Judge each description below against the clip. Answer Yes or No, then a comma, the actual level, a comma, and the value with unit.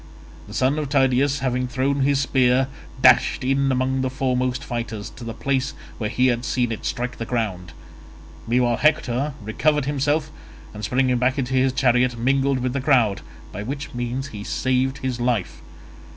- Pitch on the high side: No, low, 130 Hz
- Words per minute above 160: Yes, average, 170 wpm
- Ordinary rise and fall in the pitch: No, narrow, 2.0 semitones